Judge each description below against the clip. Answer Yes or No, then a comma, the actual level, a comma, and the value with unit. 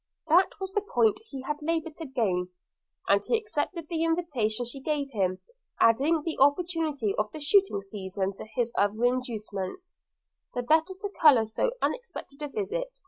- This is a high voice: Yes, very high, 285 Hz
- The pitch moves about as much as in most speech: No, wide, 7.1 semitones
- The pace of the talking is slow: No, average, 165 wpm